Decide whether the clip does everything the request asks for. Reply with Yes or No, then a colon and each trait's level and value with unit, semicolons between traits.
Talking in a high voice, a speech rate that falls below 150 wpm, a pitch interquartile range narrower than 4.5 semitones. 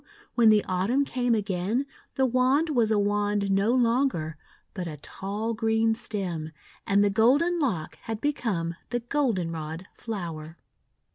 No: high, 215 Hz; average, 140 wpm; average, 4.9 semitones